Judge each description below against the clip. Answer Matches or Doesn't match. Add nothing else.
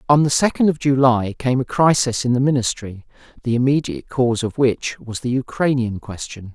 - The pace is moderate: Matches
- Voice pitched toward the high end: Doesn't match